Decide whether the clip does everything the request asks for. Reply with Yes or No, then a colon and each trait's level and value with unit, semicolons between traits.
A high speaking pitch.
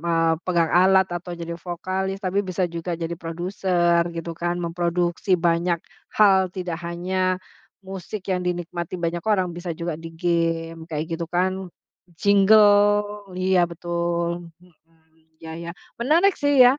No: medium, 175 Hz